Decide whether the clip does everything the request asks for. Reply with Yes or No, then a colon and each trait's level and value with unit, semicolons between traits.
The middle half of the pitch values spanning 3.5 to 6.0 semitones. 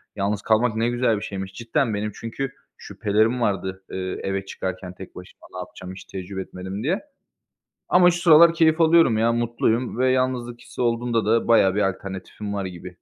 Yes: average, 4.3 semitones